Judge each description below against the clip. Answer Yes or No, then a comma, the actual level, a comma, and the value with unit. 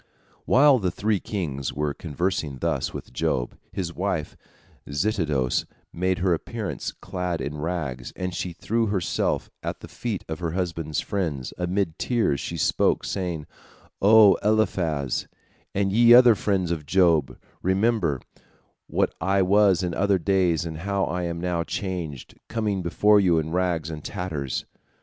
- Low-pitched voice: Yes, very low, 90 Hz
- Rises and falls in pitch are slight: No, average, 3.7 semitones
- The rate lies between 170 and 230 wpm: No, average, 150 wpm